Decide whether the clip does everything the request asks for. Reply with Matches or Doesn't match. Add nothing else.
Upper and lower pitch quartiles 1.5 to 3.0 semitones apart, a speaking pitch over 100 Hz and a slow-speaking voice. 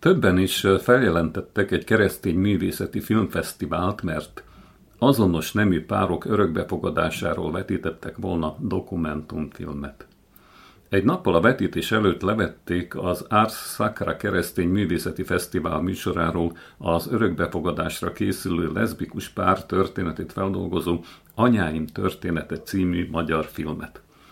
Doesn't match